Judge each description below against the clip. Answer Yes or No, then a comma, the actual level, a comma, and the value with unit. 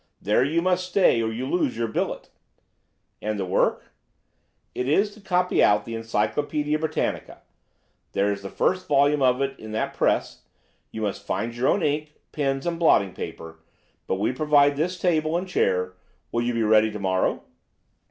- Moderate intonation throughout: No, wide, 6.4 semitones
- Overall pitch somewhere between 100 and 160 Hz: Yes, low, 135 Hz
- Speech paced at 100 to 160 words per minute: No, average, 170 wpm